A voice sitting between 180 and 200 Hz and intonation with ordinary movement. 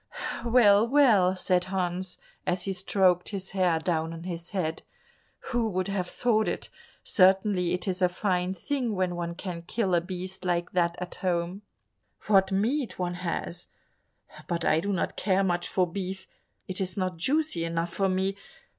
No: medium, 185 Hz; narrow, 1.9 semitones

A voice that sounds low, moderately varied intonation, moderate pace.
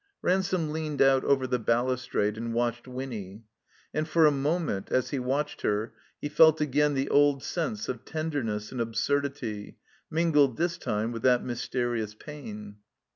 Yes: low, 130 Hz; average, 4.5 semitones; average, 155 wpm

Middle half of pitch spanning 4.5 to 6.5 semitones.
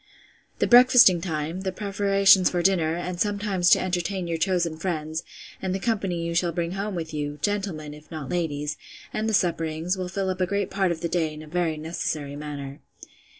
No: average, 3.4 semitones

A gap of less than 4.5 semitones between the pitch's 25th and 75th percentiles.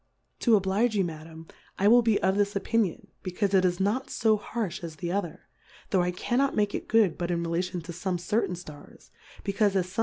Yes: average, 3.1 semitones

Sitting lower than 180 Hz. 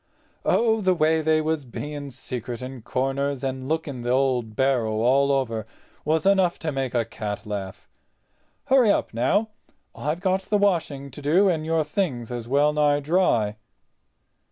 Yes: medium, 140 Hz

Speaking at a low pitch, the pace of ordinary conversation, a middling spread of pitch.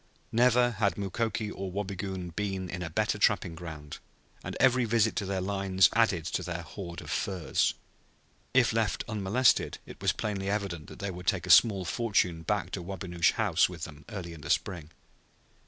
Yes: very low, 95 Hz; average, 180 wpm; average, 3.3 semitones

